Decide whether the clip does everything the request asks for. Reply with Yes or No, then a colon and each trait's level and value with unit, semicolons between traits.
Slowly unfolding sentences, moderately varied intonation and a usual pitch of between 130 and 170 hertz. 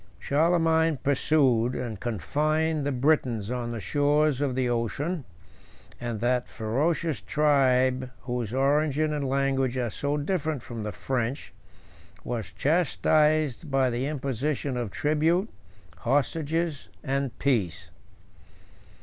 Yes: slow, 115 wpm; average, 3.8 semitones; low, 135 Hz